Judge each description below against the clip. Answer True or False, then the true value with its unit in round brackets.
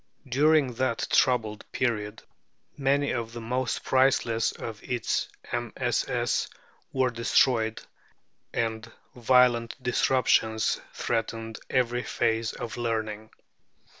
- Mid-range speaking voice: False (115 Hz)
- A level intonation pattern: True (2.2 semitones)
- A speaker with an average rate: False (95 wpm)